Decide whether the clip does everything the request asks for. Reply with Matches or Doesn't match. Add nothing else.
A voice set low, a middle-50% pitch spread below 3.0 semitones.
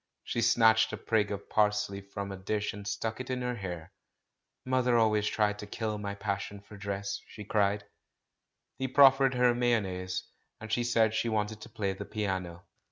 Matches